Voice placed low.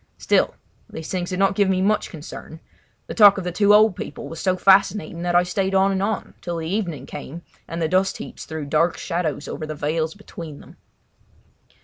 No: medium, 180 Hz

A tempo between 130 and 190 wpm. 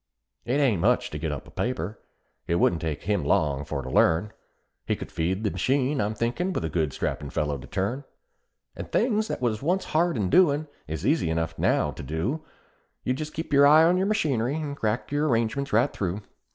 No: fast, 205 wpm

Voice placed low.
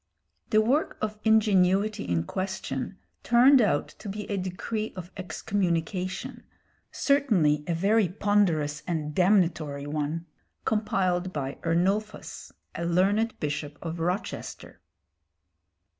No: medium, 185 Hz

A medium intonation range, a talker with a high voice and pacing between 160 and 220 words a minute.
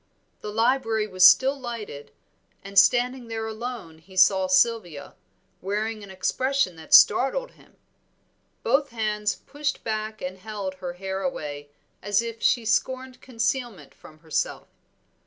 No: average, 4.5 semitones; high, 215 Hz; slow, 135 wpm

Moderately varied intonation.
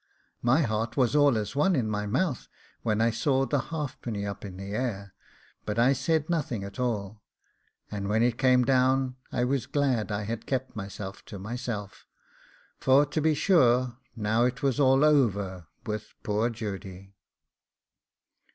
Yes: average, 4.2 semitones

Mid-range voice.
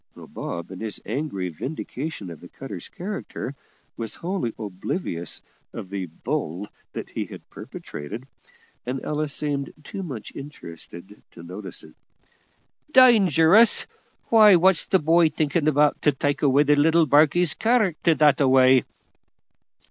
Yes: medium, 145 Hz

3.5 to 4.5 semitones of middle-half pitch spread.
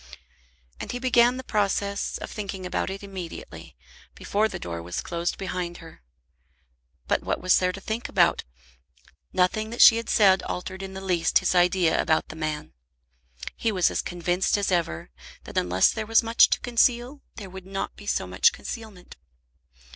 Yes: average, 3.8 semitones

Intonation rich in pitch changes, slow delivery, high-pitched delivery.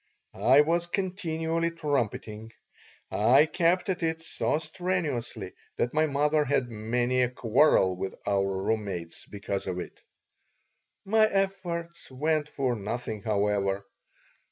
No: wide, 7.6 semitones; slow, 125 wpm; low, 135 Hz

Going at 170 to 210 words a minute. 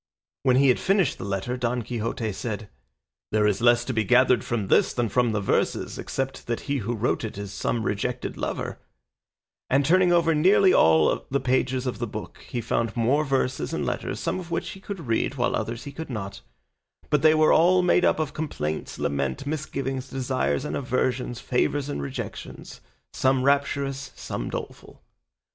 Yes: average, 185 wpm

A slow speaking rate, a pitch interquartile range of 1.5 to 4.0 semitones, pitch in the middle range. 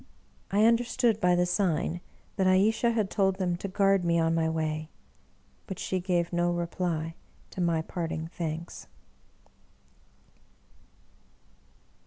Yes: slow, 125 wpm; average, 2.8 semitones; medium, 175 Hz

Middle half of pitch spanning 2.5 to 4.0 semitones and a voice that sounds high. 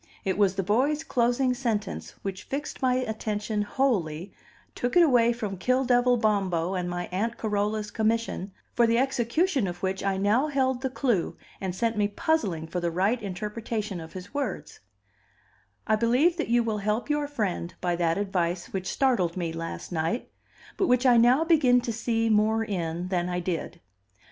No: average, 4.8 semitones; high, 215 Hz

